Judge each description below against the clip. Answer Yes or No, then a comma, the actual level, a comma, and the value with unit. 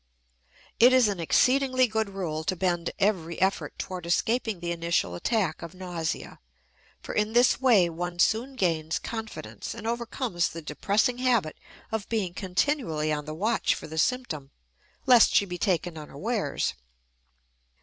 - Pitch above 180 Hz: Yes, high, 190 Hz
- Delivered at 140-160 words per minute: Yes, average, 150 wpm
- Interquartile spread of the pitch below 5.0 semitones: No, wide, 5.5 semitones